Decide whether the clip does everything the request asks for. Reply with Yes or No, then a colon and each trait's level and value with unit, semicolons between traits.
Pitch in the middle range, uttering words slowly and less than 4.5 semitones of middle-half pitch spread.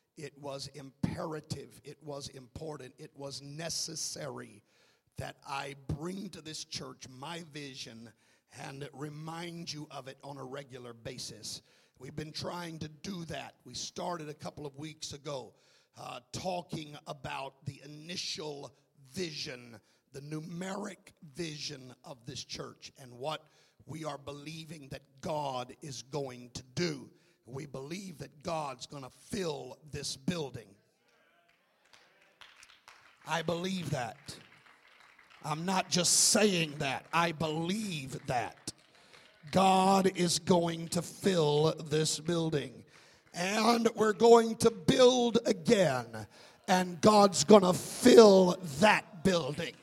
Yes: medium, 155 Hz; slow, 125 wpm; average, 4.0 semitones